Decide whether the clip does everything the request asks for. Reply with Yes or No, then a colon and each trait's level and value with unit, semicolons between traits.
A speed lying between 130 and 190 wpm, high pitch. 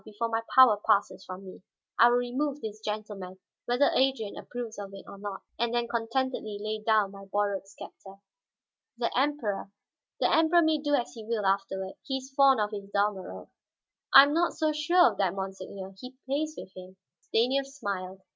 Yes: average, 185 wpm; high, 220 Hz